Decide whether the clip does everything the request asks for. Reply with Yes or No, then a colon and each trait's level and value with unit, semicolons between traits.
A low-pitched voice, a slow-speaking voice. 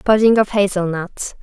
No: high, 195 Hz; slow, 125 wpm